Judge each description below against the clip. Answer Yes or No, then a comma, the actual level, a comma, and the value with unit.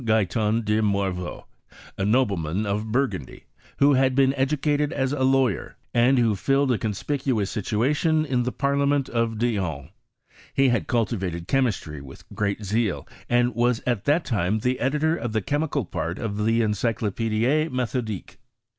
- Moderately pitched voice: No, low, 115 Hz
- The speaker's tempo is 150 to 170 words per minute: Yes, average, 155 wpm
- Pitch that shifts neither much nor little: Yes, average, 4.5 semitones